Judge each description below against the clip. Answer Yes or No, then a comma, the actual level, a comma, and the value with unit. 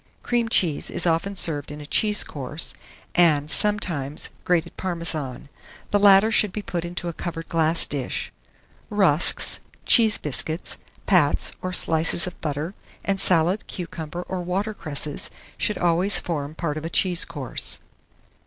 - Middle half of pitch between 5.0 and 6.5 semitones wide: No, average, 3.8 semitones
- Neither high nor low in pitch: Yes, medium, 170 Hz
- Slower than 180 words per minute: Yes, average, 145 wpm